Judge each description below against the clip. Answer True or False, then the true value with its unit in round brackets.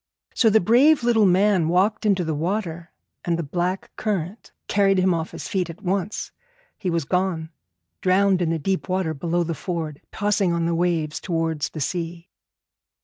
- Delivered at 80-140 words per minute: False (180 wpm)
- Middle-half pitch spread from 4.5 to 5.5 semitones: False (2.9 semitones)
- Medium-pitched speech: True (180 Hz)